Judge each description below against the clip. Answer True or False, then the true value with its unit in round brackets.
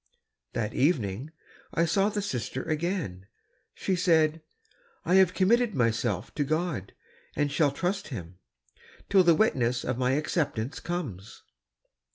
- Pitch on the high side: False (150 Hz)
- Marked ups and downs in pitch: True (6.8 semitones)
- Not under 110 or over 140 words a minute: True (135 wpm)